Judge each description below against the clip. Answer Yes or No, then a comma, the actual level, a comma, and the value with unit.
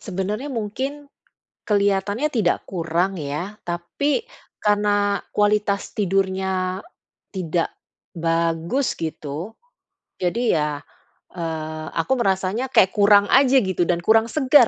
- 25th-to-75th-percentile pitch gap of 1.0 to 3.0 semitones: No, average, 3.9 semitones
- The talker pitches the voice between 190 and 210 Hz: Yes, high, 195 Hz